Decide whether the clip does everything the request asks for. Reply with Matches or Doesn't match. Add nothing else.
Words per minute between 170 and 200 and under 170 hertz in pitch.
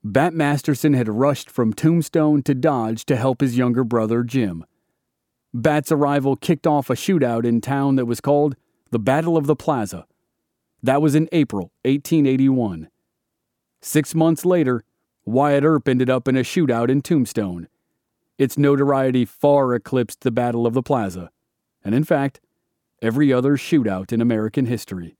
Doesn't match